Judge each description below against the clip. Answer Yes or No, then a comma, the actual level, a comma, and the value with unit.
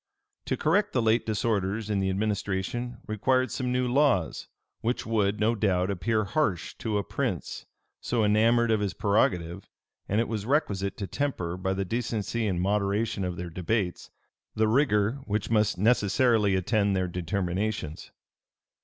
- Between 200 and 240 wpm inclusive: No, average, 155 wpm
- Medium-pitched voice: No, low, 105 Hz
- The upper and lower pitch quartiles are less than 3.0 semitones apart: No, average, 3.3 semitones